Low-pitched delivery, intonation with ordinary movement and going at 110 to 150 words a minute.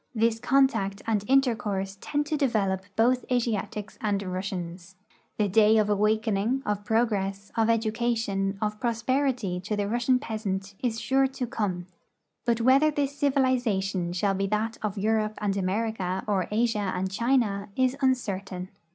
No: high, 215 Hz; average, 3.6 semitones; average, 145 wpm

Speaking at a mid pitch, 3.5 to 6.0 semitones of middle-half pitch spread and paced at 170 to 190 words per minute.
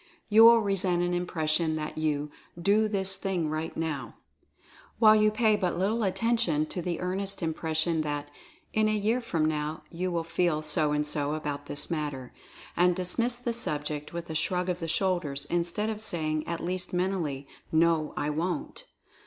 Yes: medium, 170 Hz; average, 4.2 semitones; average, 175 wpm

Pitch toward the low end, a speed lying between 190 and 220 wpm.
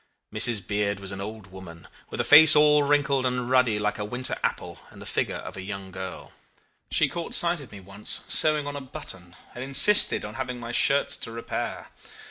Yes: low, 120 Hz; fast, 205 wpm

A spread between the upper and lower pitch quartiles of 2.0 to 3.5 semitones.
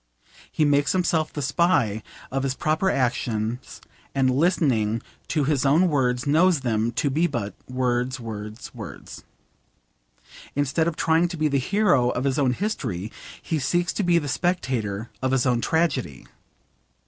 No: average, 4.8 semitones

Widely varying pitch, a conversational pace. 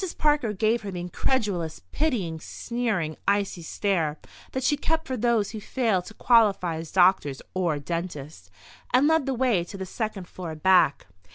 Yes: wide, 6.0 semitones; average, 165 wpm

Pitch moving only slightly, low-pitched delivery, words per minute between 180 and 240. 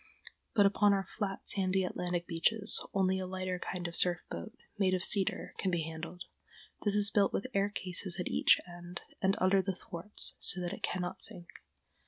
No: narrow, 1.9 semitones; medium, 185 Hz; average, 190 wpm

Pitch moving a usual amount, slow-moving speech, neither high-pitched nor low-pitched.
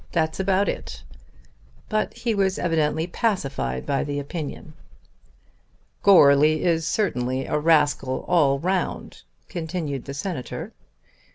Yes: average, 4.5 semitones; slow, 110 wpm; medium, 160 Hz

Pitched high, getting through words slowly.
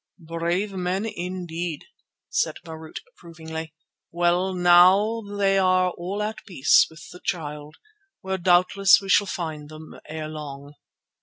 No: medium, 175 Hz; slow, 130 wpm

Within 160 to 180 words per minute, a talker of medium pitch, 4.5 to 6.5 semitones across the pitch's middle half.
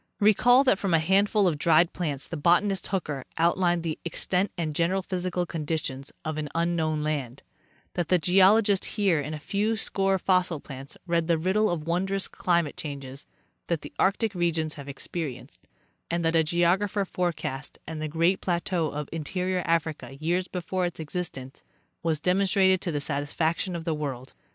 No: average, 175 wpm; medium, 170 Hz; average, 3.3 semitones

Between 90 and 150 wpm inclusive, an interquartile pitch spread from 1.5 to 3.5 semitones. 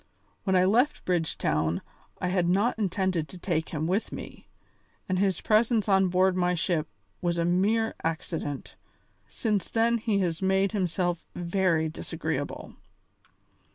Yes: average, 140 wpm; average, 2.8 semitones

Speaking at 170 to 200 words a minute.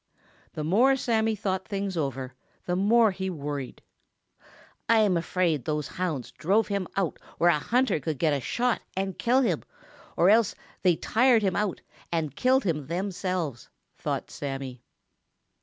No: average, 155 wpm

